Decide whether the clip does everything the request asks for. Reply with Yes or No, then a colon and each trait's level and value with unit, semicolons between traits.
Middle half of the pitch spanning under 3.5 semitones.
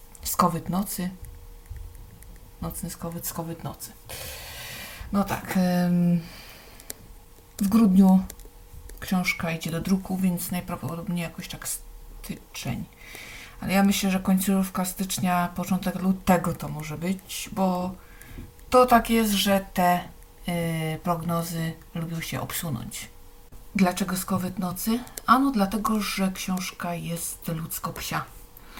Yes: narrow, 2.4 semitones